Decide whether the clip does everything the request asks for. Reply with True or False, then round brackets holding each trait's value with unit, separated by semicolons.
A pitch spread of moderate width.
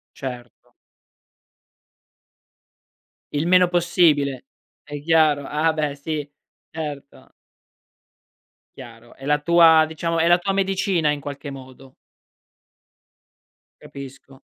True (3.2 semitones)